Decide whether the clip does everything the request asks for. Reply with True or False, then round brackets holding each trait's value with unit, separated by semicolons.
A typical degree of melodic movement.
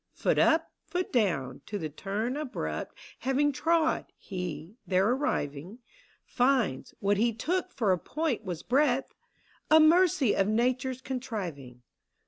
False (7.5 semitones)